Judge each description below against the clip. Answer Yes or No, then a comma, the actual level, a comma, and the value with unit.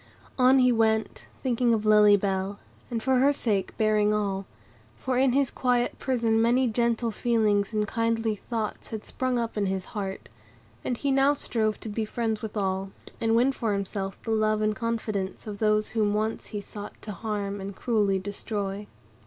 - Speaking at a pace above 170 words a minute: Yes, average, 180 wpm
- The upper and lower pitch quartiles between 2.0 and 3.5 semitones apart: Yes, narrow, 2.4 semitones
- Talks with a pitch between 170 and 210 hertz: No, high, 220 Hz